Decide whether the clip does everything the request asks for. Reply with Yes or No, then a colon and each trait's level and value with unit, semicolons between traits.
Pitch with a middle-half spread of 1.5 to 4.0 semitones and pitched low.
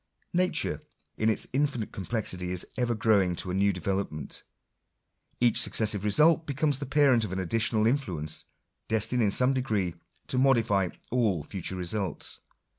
No: average, 5.0 semitones; low, 110 Hz